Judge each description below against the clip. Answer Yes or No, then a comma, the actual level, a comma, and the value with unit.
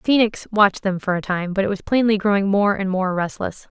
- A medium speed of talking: No, fast, 255 wpm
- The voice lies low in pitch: No, high, 200 Hz